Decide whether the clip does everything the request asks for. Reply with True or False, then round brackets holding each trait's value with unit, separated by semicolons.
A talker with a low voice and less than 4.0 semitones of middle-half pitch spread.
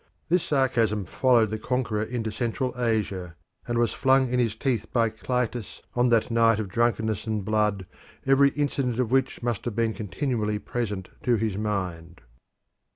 True (115 Hz; 2.8 semitones)